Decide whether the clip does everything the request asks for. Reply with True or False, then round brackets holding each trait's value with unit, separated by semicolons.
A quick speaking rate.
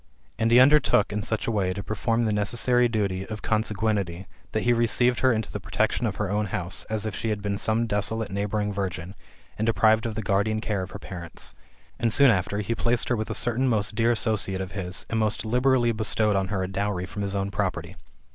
True (225 wpm)